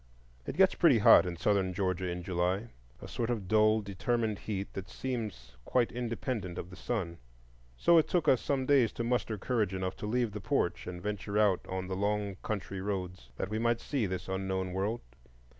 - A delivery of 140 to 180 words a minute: No, average, 190 wpm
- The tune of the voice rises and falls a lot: No, average, 3.9 semitones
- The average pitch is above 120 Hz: No, low, 100 Hz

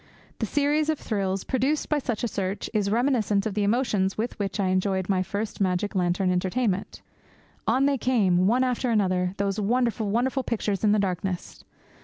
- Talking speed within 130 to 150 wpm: No, average, 180 wpm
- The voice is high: Yes, high, 205 Hz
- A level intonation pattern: No, average, 4.4 semitones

